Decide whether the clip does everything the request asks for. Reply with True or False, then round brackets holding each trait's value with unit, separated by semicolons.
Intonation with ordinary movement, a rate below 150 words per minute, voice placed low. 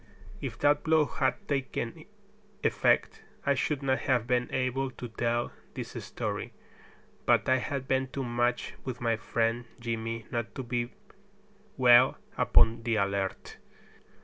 False (2.2 semitones; 140 wpm; 125 Hz)